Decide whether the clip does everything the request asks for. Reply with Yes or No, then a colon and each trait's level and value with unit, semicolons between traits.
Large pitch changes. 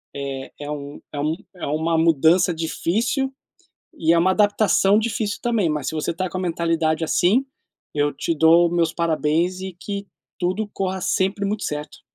No: average, 3.5 semitones